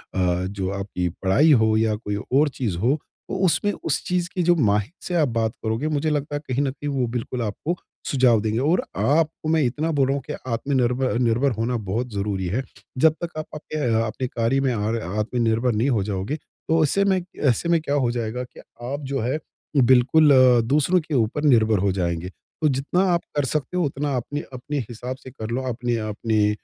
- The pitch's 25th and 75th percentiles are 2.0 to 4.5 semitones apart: No, average, 4.9 semitones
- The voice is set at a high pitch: No, low, 125 Hz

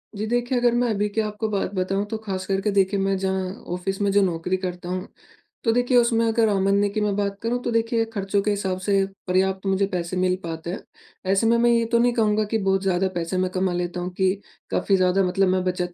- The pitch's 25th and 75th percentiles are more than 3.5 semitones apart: No, average, 2.9 semitones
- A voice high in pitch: Yes, high, 195 Hz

